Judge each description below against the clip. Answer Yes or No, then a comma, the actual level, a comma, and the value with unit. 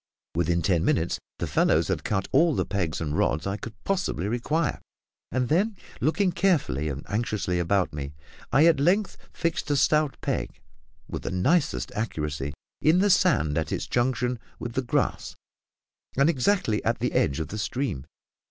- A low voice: Yes, low, 120 Hz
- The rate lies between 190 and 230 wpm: No, average, 170 wpm